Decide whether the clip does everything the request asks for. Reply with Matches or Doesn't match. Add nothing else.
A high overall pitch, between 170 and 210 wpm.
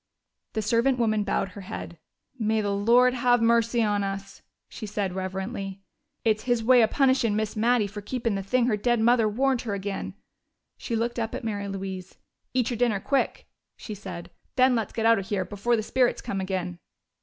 Matches